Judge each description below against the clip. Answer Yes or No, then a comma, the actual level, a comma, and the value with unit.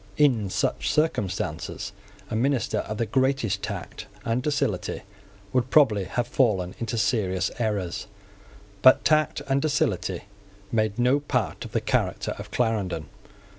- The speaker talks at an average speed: No, slow, 130 wpm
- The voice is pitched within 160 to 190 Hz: No, low, 115 Hz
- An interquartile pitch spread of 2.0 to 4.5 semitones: No, average, 5.0 semitones